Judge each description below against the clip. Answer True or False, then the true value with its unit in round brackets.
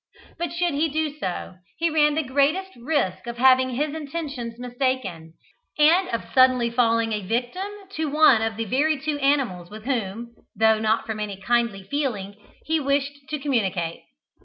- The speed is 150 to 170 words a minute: True (165 wpm)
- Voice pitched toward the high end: True (255 Hz)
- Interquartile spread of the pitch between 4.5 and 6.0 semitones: True (5.1 semitones)